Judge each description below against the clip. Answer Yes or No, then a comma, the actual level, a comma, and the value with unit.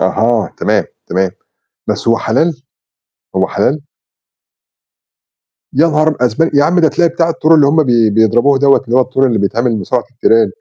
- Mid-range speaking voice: No, low, 130 Hz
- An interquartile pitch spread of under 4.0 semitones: No, average, 5.2 semitones